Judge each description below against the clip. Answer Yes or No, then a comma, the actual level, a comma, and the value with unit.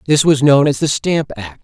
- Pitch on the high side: No, low, 135 Hz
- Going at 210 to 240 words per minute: No, fast, 255 wpm